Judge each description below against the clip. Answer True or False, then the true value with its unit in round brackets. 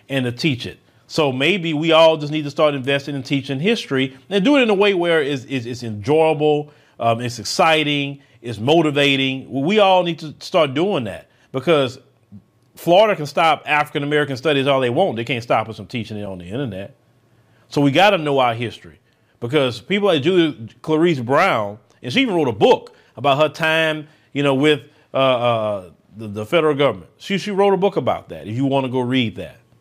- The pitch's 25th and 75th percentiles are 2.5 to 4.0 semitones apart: False (4.8 semitones)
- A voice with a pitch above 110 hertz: True (140 Hz)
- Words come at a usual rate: False (210 wpm)